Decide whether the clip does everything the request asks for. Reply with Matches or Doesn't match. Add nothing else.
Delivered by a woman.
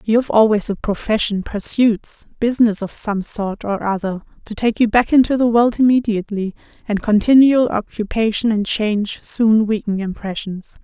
Matches